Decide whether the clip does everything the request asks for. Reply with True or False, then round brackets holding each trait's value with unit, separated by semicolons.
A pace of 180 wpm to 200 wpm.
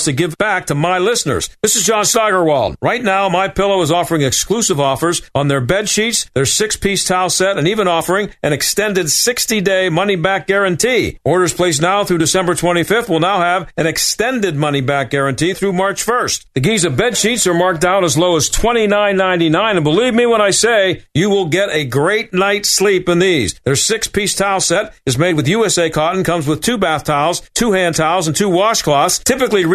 True (195 wpm)